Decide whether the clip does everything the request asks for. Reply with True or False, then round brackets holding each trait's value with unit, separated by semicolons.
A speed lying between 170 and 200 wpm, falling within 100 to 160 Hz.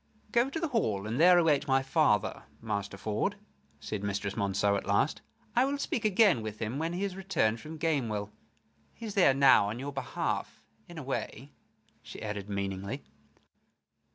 True (175 wpm; 135 Hz)